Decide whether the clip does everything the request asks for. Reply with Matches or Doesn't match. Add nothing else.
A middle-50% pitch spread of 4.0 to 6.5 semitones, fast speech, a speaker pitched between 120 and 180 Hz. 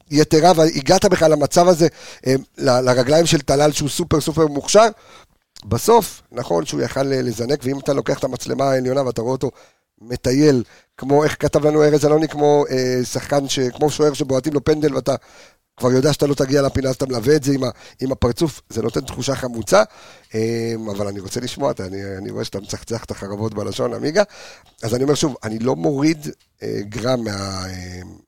Matches